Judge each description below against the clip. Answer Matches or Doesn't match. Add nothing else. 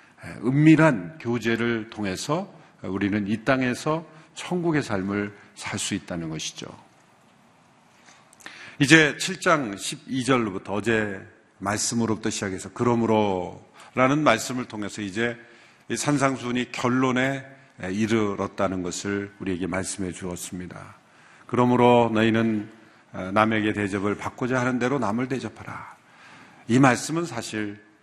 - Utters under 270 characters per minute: Matches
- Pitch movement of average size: Matches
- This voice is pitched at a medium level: Doesn't match